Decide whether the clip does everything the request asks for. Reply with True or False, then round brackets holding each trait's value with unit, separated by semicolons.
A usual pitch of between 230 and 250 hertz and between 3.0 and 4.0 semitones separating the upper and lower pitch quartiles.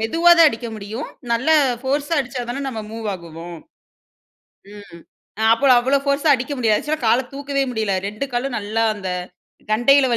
False (240 Hz; 4.4 semitones)